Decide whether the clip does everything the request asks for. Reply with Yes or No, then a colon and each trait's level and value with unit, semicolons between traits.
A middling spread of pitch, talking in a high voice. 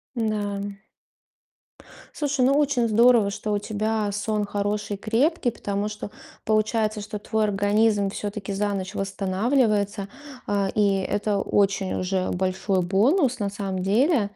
No: narrow, 1.8 semitones; high, 205 Hz